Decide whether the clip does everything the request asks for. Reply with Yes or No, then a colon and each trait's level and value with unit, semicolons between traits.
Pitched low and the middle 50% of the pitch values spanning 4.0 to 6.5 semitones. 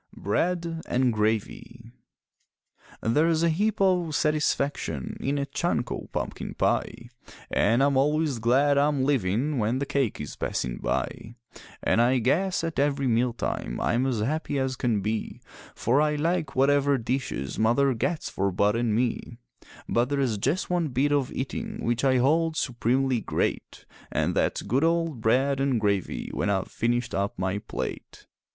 Yes: low, 130 Hz; average, 4.3 semitones